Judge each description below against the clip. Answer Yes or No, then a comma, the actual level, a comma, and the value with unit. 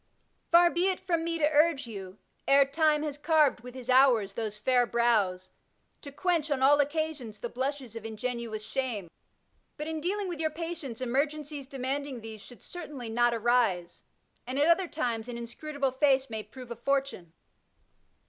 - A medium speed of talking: Yes, average, 170 wpm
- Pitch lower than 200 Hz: No, very high, 265 Hz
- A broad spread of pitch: No, average, 4.6 semitones